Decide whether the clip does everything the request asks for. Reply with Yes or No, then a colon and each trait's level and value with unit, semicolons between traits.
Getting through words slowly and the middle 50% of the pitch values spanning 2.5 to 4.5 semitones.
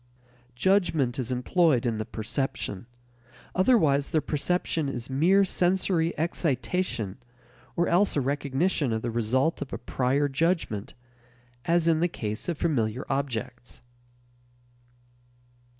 No: slow, 120 wpm; wide, 5.6 semitones